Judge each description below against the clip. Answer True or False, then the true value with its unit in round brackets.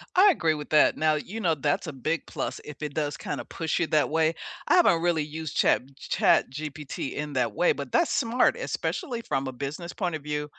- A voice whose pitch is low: False (155 Hz)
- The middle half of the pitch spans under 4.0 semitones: True (2.5 semitones)